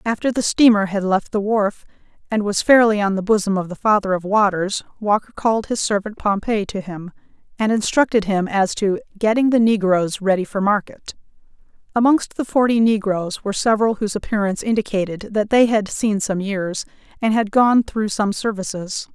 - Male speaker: No, female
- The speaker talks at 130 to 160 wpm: No, average, 180 wpm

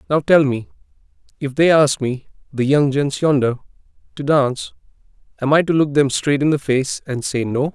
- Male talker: Yes, male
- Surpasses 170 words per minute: Yes, average, 195 wpm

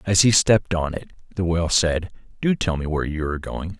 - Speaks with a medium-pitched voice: No, very low, 90 Hz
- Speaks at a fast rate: Yes, fast, 235 wpm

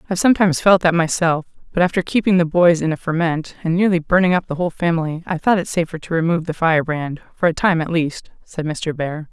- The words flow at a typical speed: No, fast, 230 wpm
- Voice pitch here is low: No, medium, 170 Hz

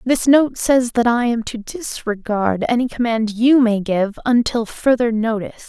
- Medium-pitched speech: No, high, 235 Hz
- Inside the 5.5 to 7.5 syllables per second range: No, 4.4 syllables/s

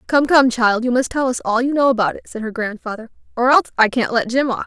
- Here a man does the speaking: No, female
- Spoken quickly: Yes, fast, 285 wpm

